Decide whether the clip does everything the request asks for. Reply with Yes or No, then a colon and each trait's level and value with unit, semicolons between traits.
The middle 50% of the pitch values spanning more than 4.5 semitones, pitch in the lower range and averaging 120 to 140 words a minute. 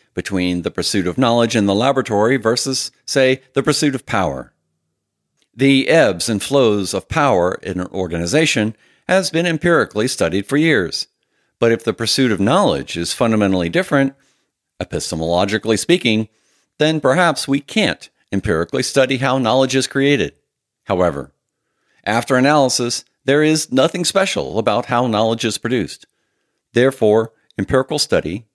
Yes: average, 5.0 semitones; low, 120 Hz; slow, 135 wpm